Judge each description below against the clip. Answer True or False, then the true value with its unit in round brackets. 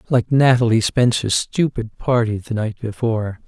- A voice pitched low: True (115 Hz)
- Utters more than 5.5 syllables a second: False (4.7 syllables/s)